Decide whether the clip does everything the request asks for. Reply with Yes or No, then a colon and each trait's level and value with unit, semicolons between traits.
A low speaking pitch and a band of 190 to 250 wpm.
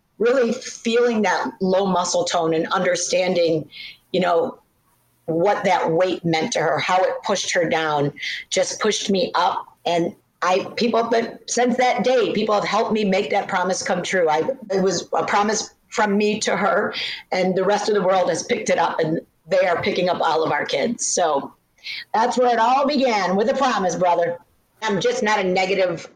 No: high, 195 Hz; average, 195 wpm